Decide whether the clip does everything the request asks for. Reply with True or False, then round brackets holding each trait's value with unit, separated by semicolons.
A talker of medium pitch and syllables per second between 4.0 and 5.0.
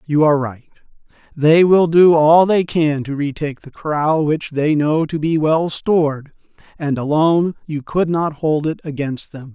True (155 Hz; 4.5 syllables/s)